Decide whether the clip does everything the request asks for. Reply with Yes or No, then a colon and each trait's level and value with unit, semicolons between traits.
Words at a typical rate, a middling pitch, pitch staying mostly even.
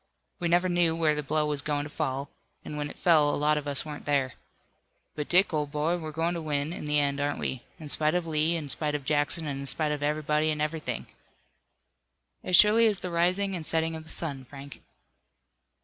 No: fast, 225 wpm; medium, 150 Hz; narrow, 2.2 semitones